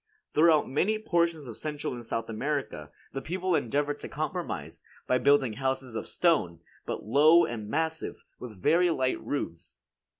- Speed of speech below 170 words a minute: Yes, average, 155 wpm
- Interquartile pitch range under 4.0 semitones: No, average, 5.3 semitones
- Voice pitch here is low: No, medium, 145 Hz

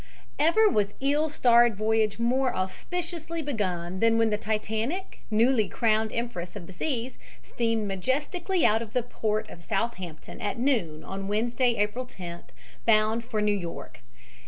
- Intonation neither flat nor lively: Yes, average, 3.7 semitones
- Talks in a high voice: Yes, high, 225 Hz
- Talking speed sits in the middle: Yes, average, 150 wpm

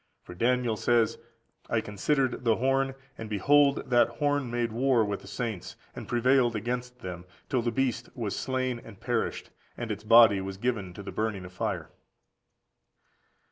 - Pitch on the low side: Yes, low, 120 Hz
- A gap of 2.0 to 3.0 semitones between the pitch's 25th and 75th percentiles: No, average, 3.5 semitones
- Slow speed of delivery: No, average, 165 wpm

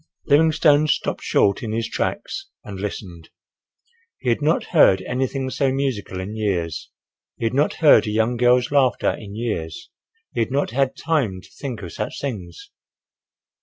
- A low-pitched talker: Yes, low, 120 Hz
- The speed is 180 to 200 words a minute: No, average, 155 wpm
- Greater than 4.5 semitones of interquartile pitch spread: Yes, wide, 5.6 semitones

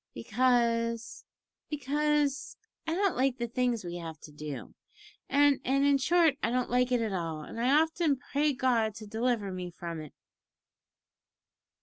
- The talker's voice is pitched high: Yes, high, 245 Hz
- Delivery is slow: No, average, 165 wpm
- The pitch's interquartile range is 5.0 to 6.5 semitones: Yes, average, 5.3 semitones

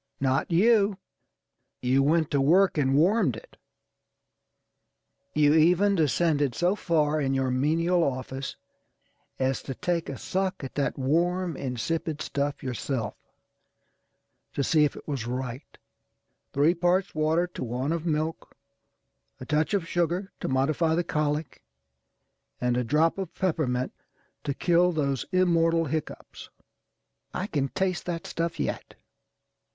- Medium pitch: Yes, medium, 155 Hz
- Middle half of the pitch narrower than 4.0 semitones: No, average, 4.3 semitones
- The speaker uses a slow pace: Yes, slow, 130 wpm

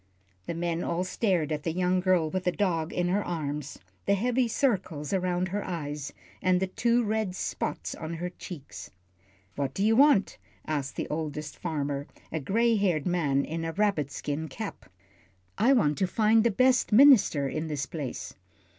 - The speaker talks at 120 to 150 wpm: No, average, 175 wpm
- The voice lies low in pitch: No, medium, 175 Hz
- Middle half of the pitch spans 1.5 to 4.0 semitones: No, average, 5.0 semitones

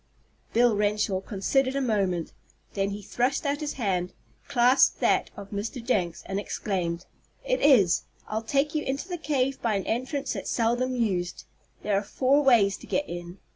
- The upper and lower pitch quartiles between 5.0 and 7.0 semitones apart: Yes, wide, 5.5 semitones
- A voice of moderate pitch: No, high, 225 Hz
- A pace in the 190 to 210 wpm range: No, average, 175 wpm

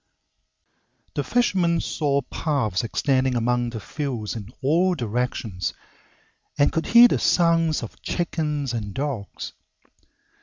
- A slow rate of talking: Yes, slow, 115 wpm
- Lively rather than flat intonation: Yes, wide, 5.7 semitones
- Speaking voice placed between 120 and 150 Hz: Yes, medium, 140 Hz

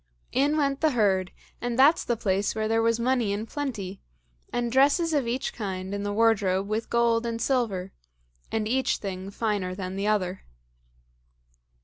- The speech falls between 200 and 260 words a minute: No, average, 165 wpm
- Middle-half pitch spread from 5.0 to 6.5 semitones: No, average, 3.7 semitones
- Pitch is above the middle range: Yes, high, 225 Hz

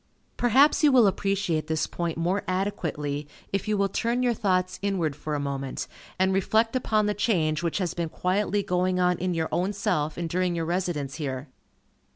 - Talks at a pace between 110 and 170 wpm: No, average, 190 wpm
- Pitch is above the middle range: No, medium, 180 Hz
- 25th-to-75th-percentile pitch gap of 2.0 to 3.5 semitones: No, average, 4.1 semitones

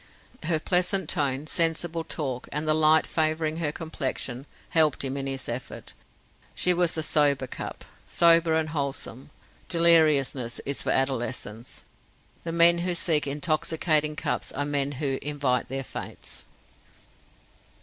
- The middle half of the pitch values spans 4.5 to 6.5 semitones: No, average, 3.2 semitones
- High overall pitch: No, medium, 150 Hz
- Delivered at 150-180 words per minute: No, slow, 135 wpm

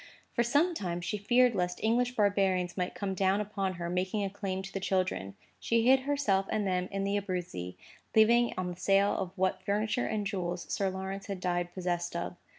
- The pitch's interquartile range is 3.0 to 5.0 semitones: No, narrow, 2.6 semitones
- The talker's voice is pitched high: Yes, high, 195 Hz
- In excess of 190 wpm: Yes, average, 200 wpm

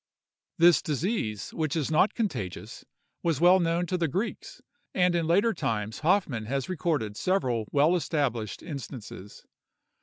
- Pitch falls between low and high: Yes, medium, 160 Hz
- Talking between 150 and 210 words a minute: No, average, 140 wpm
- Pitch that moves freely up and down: Yes, wide, 6.4 semitones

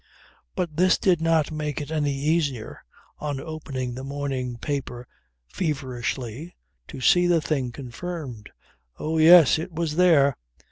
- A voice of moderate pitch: Yes, medium, 150 Hz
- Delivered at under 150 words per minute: Yes, slow, 135 wpm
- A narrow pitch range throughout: No, average, 3.8 semitones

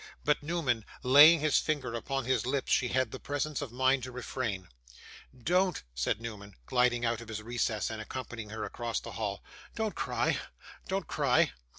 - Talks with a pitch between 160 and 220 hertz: No, low, 125 Hz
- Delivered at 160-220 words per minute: Yes, average, 175 wpm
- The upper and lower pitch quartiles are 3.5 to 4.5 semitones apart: Yes, average, 4.0 semitones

